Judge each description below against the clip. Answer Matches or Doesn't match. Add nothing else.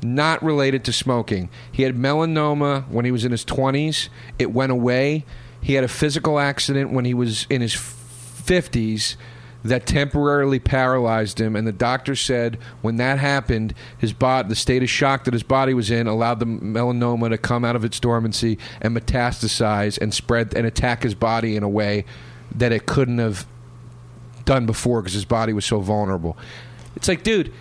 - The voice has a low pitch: Matches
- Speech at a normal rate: Matches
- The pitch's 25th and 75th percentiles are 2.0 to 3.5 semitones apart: Matches